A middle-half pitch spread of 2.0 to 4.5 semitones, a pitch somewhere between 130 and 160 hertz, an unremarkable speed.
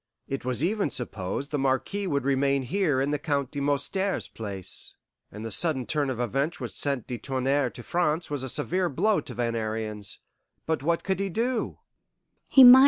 No: average, 5.0 semitones; medium, 140 Hz; average, 180 wpm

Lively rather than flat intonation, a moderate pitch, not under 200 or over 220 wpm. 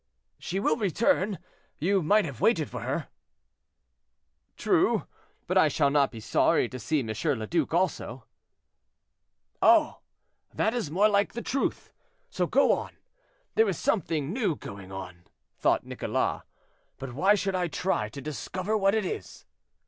No: wide, 6.6 semitones; medium, 175 Hz; average, 150 wpm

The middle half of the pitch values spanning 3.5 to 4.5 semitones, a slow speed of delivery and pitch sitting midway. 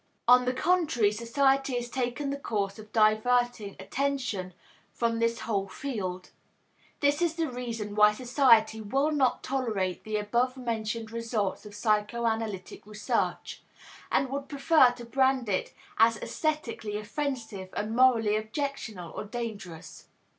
No: average, 3.8 semitones; slow, 130 wpm; high, 230 Hz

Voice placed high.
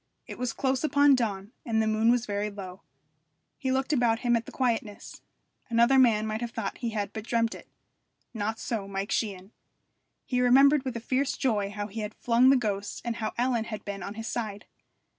Yes: high, 225 Hz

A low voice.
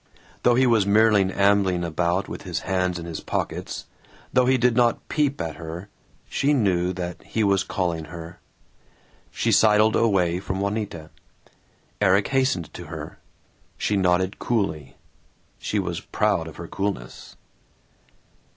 Yes: very low, 95 Hz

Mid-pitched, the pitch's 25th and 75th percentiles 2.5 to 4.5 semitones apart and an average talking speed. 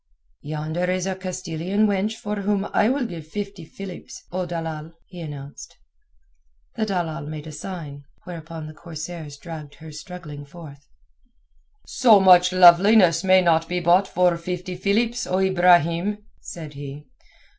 Yes: medium, 175 Hz; average, 3.2 semitones; average, 145 wpm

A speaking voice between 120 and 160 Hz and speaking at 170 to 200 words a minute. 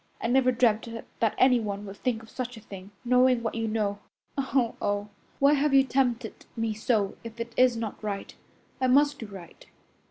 No: high, 230 Hz; average, 190 wpm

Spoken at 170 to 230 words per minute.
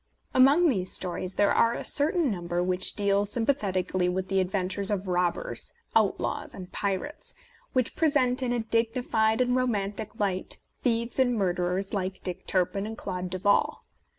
No: average, 155 wpm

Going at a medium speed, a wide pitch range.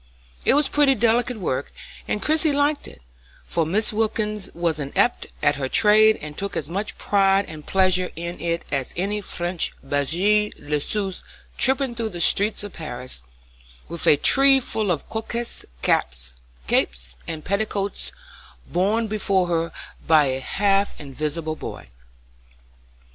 Yes: average, 145 wpm; wide, 5.7 semitones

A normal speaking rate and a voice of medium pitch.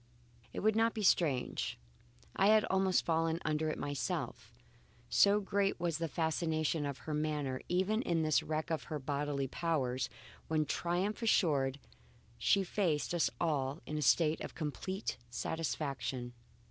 Yes: average, 145 wpm; medium, 160 Hz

